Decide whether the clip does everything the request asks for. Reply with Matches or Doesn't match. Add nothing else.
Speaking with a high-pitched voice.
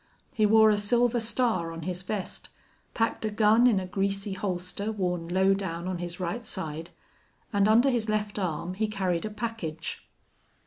Matches